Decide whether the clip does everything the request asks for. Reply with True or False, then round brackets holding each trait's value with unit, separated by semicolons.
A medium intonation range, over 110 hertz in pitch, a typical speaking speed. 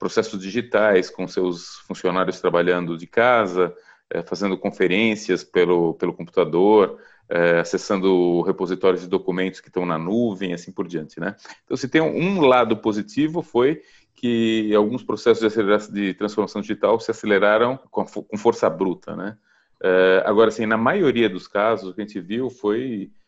False (3.7 semitones; 100 Hz; 145 wpm)